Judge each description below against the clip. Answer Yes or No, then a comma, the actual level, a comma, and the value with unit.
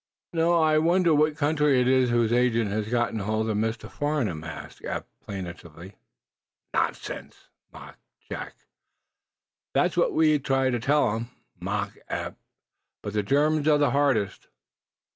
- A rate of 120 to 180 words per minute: Yes, average, 145 wpm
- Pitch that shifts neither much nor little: No, wide, 5.8 semitones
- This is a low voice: Yes, low, 125 Hz